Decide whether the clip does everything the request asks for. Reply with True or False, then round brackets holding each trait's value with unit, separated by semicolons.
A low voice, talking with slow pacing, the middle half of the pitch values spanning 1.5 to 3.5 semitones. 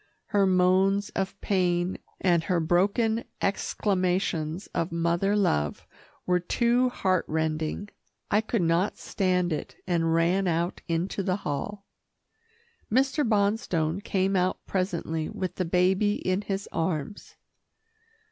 False (185 Hz; 120 wpm; 3.1 semitones)